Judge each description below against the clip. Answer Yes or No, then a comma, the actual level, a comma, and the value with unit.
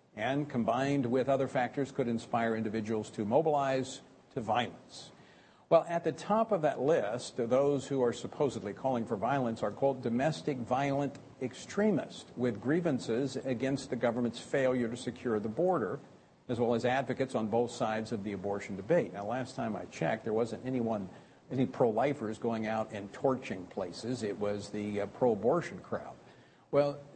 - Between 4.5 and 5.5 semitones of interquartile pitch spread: No, average, 3.8 semitones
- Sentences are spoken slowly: No, average, 175 wpm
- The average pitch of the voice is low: Yes, low, 125 Hz